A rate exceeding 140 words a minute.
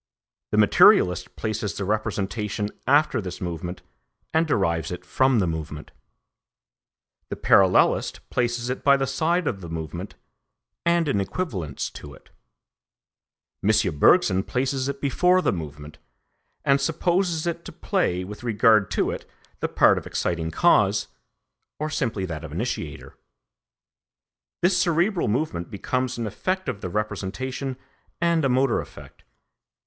No: slow, 135 wpm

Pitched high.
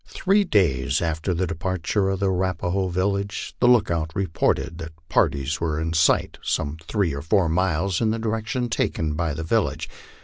No: very low, 90 Hz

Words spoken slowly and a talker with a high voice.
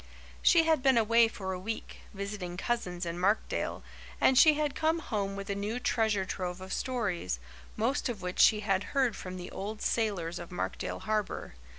No: average, 185 wpm; high, 210 Hz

